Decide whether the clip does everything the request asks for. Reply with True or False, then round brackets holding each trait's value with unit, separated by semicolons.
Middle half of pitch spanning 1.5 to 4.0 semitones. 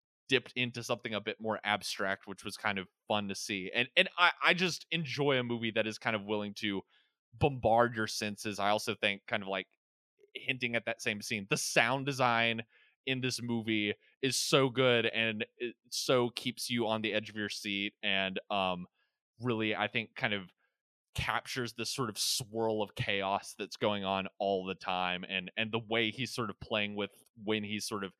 True (3.0 semitones)